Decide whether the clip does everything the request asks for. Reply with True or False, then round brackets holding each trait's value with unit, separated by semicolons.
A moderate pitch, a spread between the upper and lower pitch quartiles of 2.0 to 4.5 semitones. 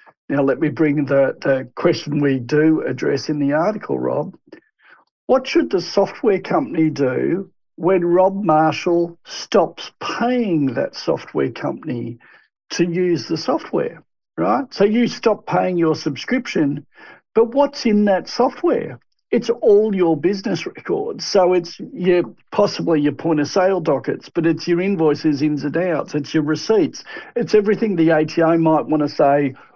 False (170 Hz; 5.6 semitones)